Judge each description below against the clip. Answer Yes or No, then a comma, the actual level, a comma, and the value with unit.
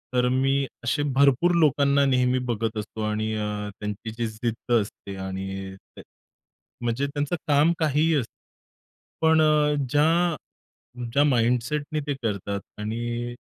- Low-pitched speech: Yes, low, 125 Hz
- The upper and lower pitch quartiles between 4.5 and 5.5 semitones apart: Yes, average, 5.0 semitones